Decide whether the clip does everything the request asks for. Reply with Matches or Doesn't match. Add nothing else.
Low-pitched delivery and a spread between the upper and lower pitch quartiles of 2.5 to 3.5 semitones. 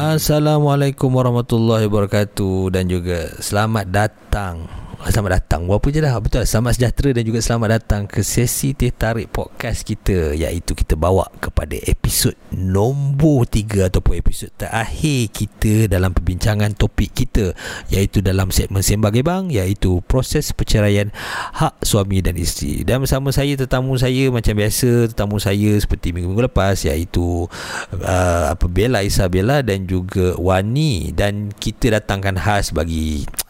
Doesn't match